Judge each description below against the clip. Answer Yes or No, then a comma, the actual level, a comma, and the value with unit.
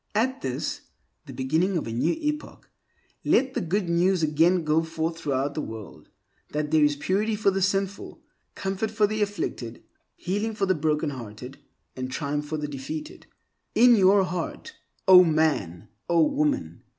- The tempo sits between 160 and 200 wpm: Yes, average, 165 wpm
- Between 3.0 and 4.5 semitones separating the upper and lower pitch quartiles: No, average, 5.3 semitones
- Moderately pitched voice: Yes, medium, 165 Hz